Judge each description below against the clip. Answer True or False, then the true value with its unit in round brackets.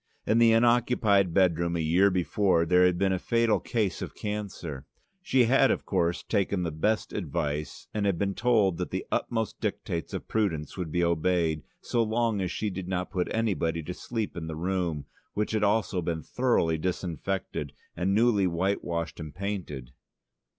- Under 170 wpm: False (180 wpm)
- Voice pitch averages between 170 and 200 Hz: False (95 Hz)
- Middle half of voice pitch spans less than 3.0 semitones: False (4.1 semitones)